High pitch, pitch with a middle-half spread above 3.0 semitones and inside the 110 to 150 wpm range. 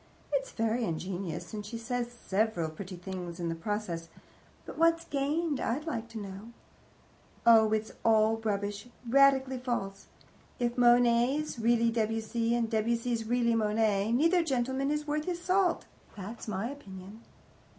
Yes: high, 230 Hz; average, 3.9 semitones; average, 140 wpm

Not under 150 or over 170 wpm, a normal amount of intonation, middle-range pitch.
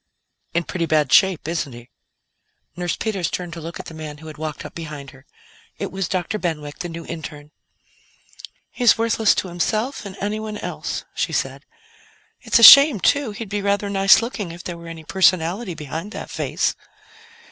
No: average, 180 wpm; average, 4.5 semitones; medium, 175 Hz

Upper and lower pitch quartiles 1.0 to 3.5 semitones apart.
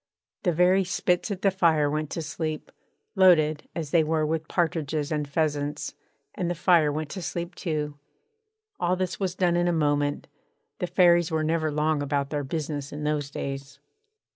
Yes: average, 2.8 semitones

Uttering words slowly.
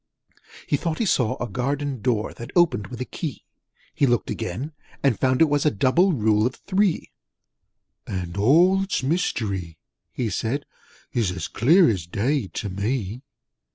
No: average, 155 wpm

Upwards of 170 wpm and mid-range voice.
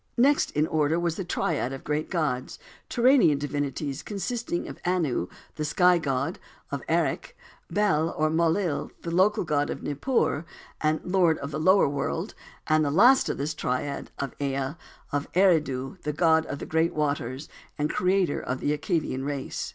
No: average, 165 wpm; medium, 155 Hz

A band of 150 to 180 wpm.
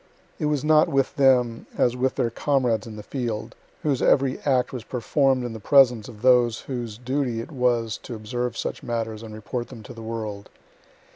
No: average, 195 wpm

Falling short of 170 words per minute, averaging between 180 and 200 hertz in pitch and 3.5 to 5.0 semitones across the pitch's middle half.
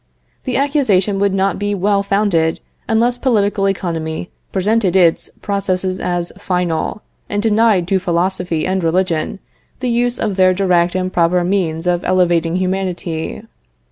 No: average, 140 wpm; medium, 185 Hz; average, 2.7 semitones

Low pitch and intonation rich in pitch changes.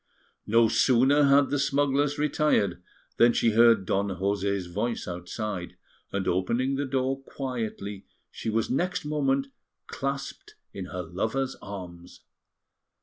Yes: low, 115 Hz; wide, 5.7 semitones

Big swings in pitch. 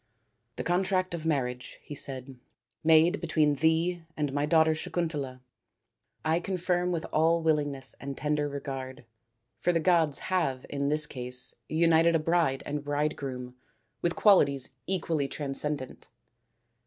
No: average, 3.4 semitones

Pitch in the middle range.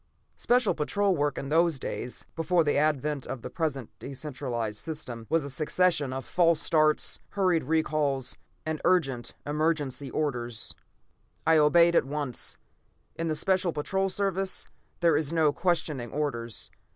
Yes: medium, 150 Hz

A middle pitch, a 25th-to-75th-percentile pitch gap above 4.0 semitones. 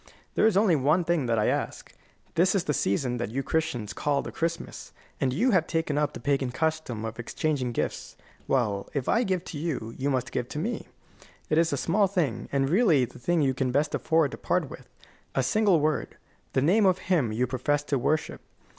Yes: medium, 145 Hz; average, 4.8 semitones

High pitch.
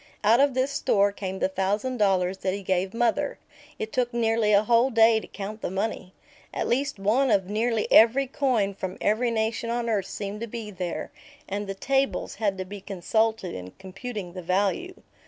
Yes: high, 215 Hz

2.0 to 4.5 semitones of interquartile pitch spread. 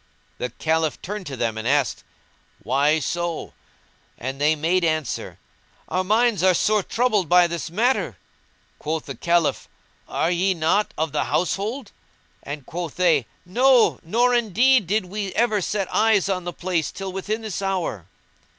No: average, 5.0 semitones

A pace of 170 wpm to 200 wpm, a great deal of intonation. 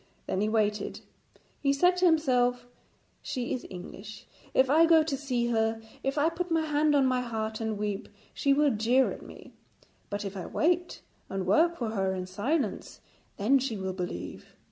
Yes: average, 185 wpm; wide, 5.9 semitones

